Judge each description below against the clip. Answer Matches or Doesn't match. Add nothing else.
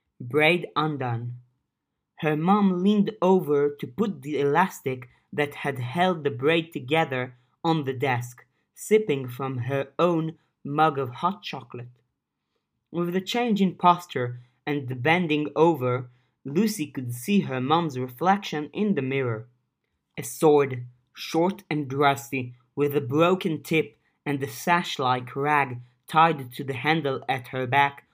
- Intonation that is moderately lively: Matches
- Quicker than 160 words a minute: Doesn't match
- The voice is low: Doesn't match